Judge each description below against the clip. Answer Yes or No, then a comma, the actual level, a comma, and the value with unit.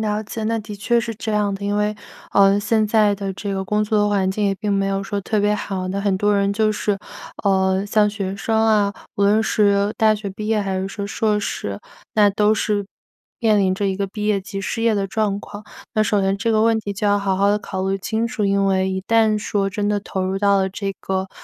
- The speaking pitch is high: Yes, high, 205 Hz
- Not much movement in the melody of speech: Yes, narrow, 1.4 semitones